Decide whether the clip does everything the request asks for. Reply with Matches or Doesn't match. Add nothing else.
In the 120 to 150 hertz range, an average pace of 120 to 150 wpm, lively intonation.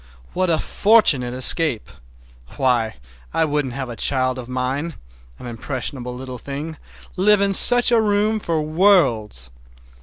Matches